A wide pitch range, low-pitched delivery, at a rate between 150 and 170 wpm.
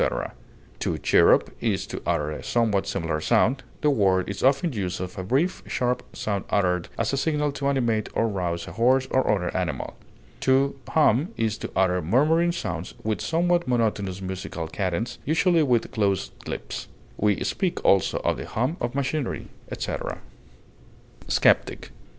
Yes: wide, 6.8 semitones; low, 115 Hz; average, 155 wpm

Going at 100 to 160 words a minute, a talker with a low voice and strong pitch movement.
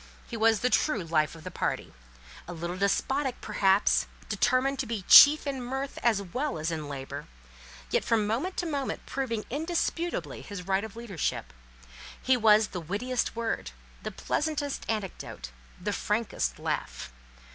No: average, 155 wpm; high, 225 Hz; wide, 6.5 semitones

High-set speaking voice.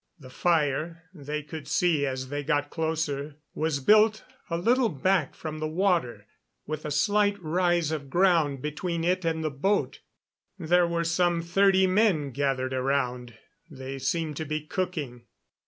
No: medium, 160 Hz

